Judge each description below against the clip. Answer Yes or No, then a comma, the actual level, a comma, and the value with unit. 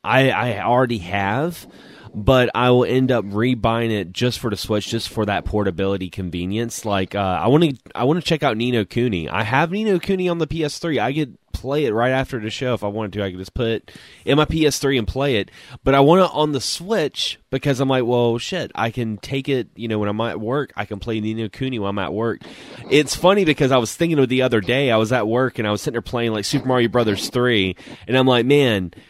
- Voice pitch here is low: Yes, low, 120 Hz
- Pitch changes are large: No, average, 4.2 semitones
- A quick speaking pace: Yes, fast, 255 wpm